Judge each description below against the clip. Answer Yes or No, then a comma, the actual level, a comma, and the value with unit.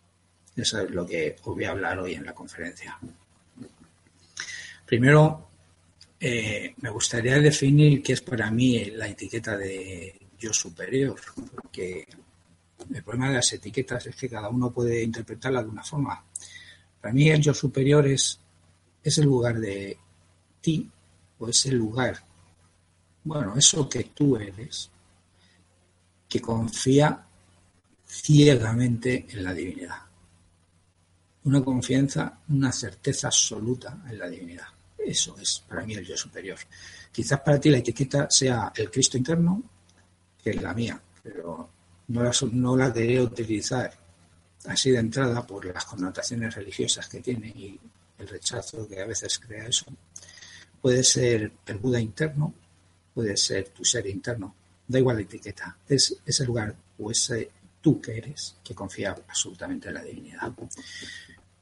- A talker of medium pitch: No, low, 115 Hz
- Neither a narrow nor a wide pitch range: No, wide, 6.3 semitones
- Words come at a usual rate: Yes, average, 145 wpm